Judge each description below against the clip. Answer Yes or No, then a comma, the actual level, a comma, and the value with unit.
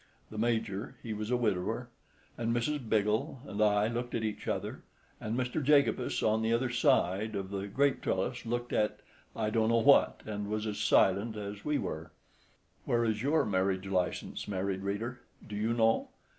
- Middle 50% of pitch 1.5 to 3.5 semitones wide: Yes, average, 2.7 semitones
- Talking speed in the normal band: Yes, average, 170 wpm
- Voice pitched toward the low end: Yes, low, 110 Hz